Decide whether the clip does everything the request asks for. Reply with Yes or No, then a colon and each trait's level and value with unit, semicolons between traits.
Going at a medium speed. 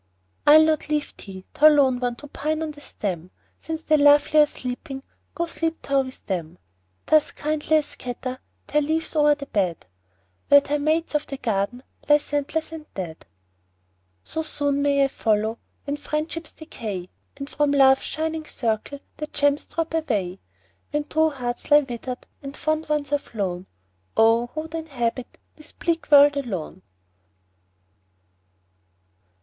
Yes: average, 155 wpm